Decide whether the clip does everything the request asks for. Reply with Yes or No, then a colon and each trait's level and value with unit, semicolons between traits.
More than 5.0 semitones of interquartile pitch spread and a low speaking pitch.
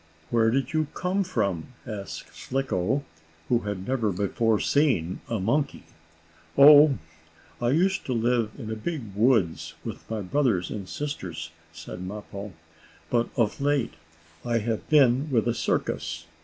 Yes: wide, 5.6 semitones; low, 115 Hz